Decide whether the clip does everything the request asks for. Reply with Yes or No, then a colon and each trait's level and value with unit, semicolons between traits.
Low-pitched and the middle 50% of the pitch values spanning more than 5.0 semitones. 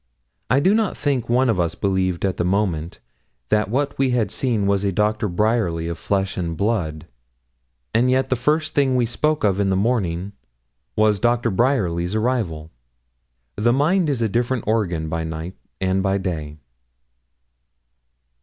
Yes: low, 105 Hz; wide, 5.5 semitones